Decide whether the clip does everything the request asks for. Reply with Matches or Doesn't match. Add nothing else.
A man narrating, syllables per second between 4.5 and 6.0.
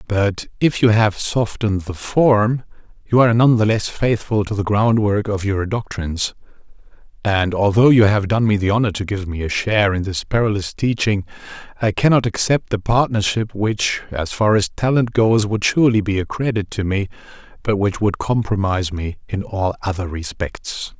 Matches